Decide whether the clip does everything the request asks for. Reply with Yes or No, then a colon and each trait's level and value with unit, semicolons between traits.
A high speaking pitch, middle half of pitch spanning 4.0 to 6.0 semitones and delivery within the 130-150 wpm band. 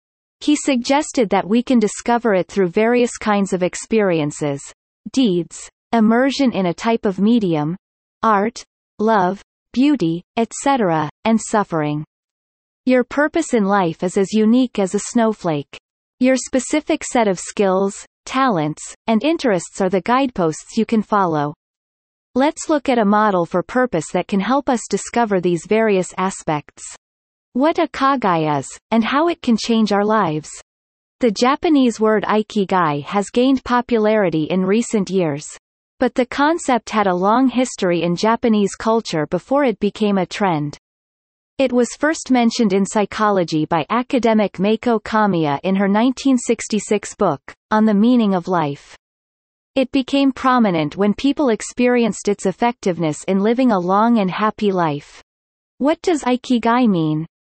Yes: high, 215 Hz; average, 4.9 semitones; average, 145 wpm